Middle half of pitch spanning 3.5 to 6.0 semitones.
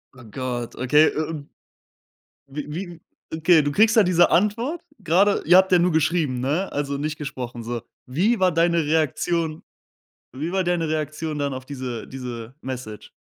Yes: average, 5.1 semitones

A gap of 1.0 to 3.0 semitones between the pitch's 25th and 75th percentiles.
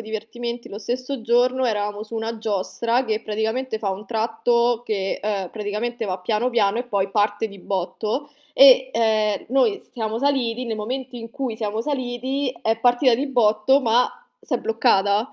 Yes: average, 2.7 semitones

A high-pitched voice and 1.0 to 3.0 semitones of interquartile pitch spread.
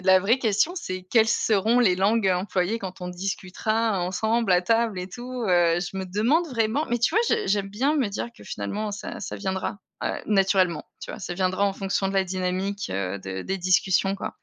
No: high, 195 Hz; average, 3.4 semitones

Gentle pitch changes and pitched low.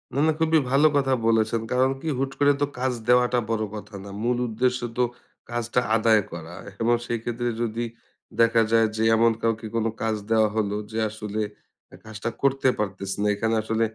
Yes: narrow, 2.2 semitones; low, 115 Hz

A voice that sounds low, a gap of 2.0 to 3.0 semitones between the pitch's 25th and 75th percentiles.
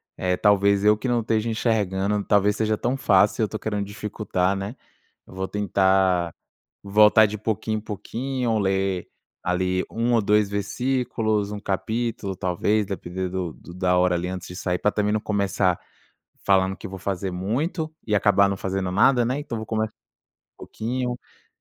Yes: low, 100 Hz; narrow, 2.6 semitones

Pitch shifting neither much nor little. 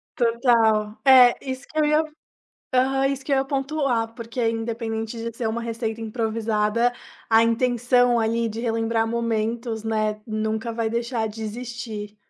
No: narrow, 1.8 semitones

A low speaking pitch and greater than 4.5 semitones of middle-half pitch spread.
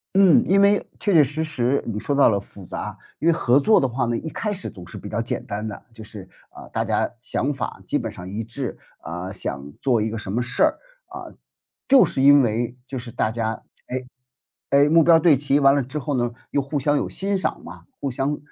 Yes: low, 130 Hz; average, 4.9 semitones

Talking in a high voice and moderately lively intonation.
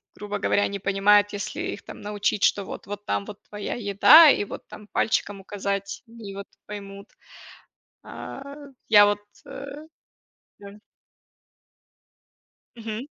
No: high, 205 Hz; narrow, 0.9 semitones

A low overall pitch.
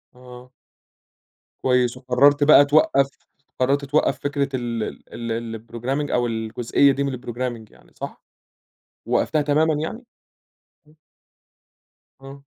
Yes: low, 130 Hz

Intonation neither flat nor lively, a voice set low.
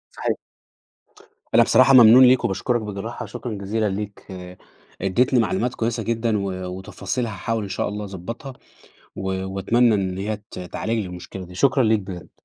Yes: average, 3.4 semitones; low, 105 Hz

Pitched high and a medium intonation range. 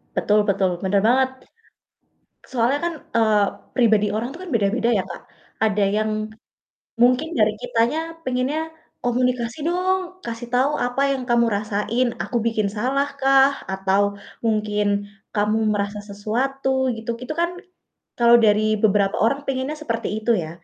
Yes: high, 235 Hz; average, 3.7 semitones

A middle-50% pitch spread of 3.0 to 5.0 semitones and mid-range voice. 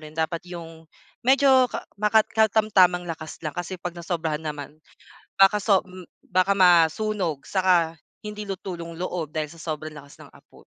Yes: average, 3.6 semitones; medium, 175 Hz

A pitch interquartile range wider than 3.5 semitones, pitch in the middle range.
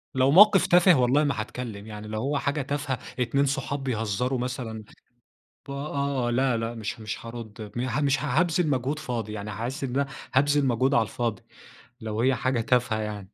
No: average, 3.9 semitones; low, 125 Hz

